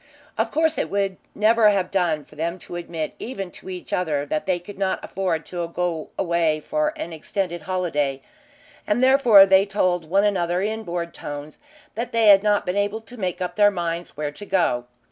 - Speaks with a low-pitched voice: No, medium, 185 Hz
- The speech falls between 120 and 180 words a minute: No, average, 200 wpm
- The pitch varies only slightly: No, average, 3.4 semitones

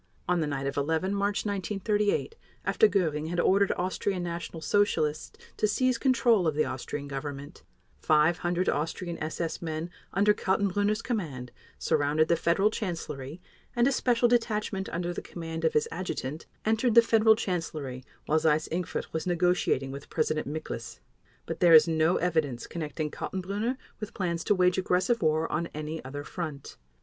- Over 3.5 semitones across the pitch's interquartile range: Yes, average, 4.7 semitones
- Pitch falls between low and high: Yes, medium, 170 Hz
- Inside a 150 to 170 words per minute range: Yes, average, 160 wpm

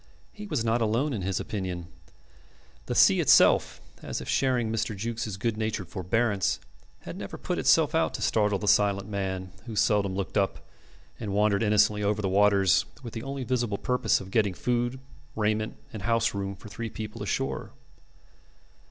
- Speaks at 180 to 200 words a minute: No, average, 170 wpm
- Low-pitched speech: Yes, low, 105 Hz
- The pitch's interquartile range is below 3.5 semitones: Yes, average, 2.7 semitones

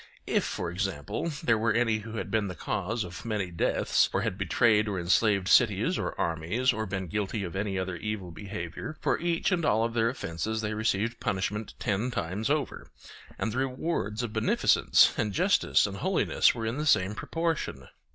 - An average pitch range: Yes, average, 3.4 semitones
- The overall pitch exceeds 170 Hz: No, low, 105 Hz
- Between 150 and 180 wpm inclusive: No, average, 190 wpm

